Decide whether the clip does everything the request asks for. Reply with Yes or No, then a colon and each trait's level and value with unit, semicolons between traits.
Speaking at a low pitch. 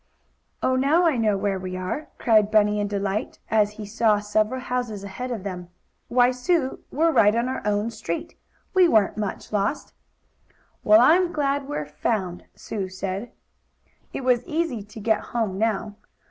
No: high, 220 Hz